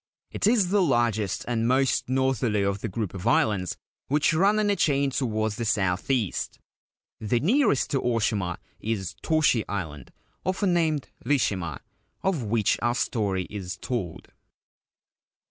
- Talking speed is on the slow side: No, average, 145 wpm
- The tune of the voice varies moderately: No, wide, 6.0 semitones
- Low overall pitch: Yes, low, 115 Hz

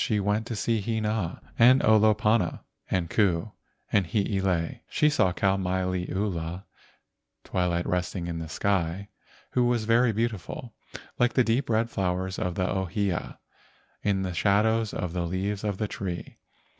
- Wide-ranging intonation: No, average, 3.4 semitones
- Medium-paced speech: Yes, average, 150 wpm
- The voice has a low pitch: Yes, low, 100 Hz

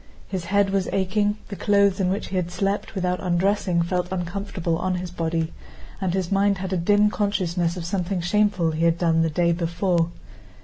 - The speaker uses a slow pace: No, average, 190 wpm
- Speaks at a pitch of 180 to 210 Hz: Yes, medium, 185 Hz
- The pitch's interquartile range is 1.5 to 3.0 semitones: Yes, narrow, 2.6 semitones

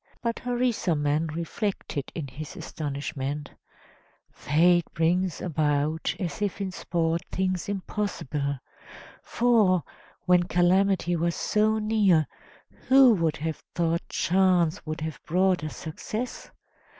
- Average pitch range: Yes, average, 4.0 semitones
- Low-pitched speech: No, medium, 175 Hz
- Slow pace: Yes, slow, 110 wpm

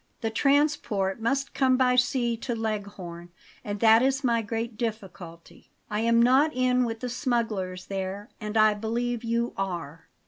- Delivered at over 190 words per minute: No, average, 160 wpm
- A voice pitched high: Yes, high, 225 Hz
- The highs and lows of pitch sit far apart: No, average, 3.6 semitones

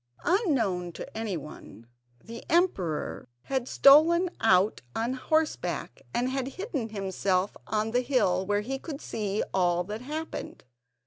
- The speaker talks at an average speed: No, slow, 130 wpm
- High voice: Yes, high, 225 Hz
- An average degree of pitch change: No, wide, 6.5 semitones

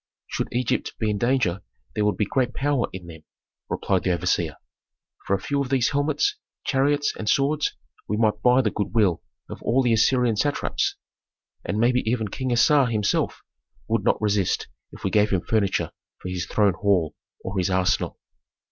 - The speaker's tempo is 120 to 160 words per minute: No, average, 180 wpm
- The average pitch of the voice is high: No, low, 110 Hz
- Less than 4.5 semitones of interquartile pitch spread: No, average, 4.8 semitones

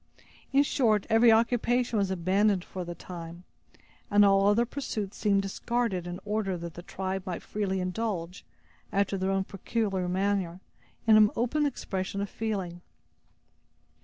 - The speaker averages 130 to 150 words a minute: Yes, average, 145 wpm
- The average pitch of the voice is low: No, high, 195 Hz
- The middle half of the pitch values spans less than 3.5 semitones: Yes, average, 3.1 semitones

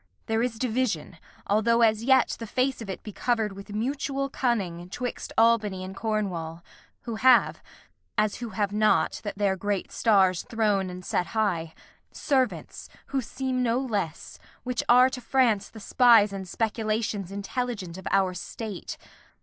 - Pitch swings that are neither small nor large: Yes, average, 3.8 semitones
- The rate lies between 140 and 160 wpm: Yes, average, 155 wpm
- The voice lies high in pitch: Yes, high, 215 Hz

